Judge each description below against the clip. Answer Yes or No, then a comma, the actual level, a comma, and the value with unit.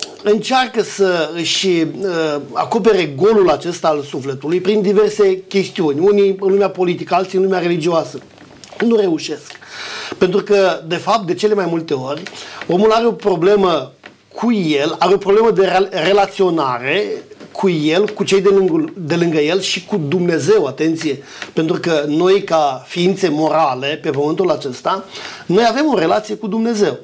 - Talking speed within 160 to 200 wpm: No, average, 150 wpm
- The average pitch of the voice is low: No, high, 190 Hz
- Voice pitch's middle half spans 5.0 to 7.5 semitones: No, average, 3.9 semitones